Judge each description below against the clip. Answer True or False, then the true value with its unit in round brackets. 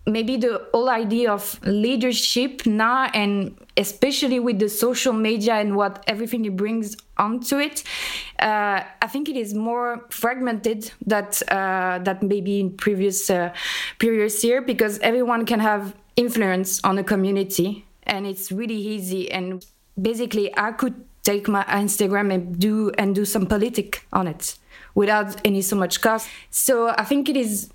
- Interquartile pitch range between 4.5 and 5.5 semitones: False (2.9 semitones)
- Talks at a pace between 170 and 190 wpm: False (160 wpm)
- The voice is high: True (215 Hz)